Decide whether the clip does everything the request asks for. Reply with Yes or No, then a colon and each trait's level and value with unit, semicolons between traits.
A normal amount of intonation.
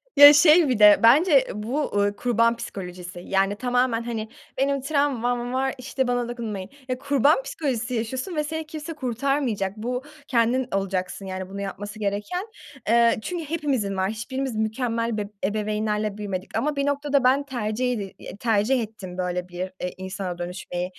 Yes: average, 4.8 semitones